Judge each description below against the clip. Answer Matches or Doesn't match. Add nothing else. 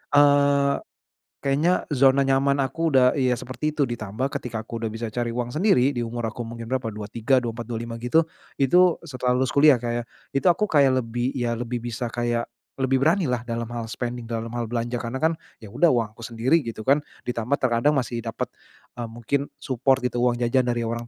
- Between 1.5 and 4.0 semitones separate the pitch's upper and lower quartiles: Matches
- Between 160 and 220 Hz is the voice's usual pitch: Doesn't match